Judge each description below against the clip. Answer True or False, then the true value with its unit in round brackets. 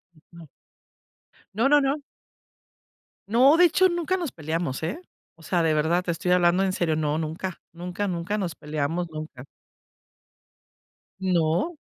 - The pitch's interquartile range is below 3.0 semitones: False (4.8 semitones)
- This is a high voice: False (175 Hz)